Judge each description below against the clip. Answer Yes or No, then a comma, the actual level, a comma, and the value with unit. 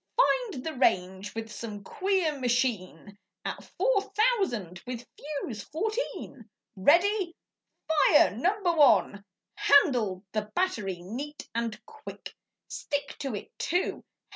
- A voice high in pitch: Yes, very high, 265 Hz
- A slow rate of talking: Yes, slow, 115 wpm